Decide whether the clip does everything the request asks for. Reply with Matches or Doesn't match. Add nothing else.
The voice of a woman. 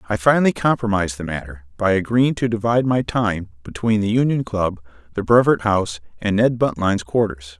Doesn't match